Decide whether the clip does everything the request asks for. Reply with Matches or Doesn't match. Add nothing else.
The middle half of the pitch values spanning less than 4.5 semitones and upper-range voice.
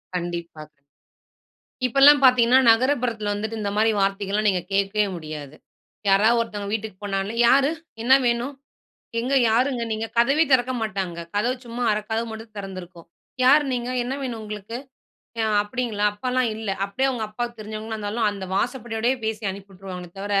Matches